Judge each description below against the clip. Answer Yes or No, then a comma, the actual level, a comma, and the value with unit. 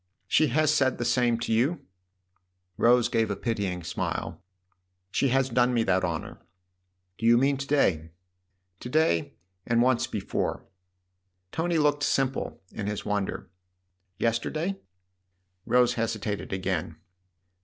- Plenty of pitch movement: Yes, wide, 6.2 semitones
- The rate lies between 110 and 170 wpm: Yes, average, 150 wpm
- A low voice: Yes, low, 115 Hz